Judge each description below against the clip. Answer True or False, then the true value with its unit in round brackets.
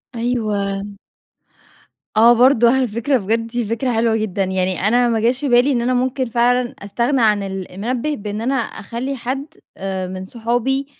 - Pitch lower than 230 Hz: False (235 Hz)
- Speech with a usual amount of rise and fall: True (3.3 semitones)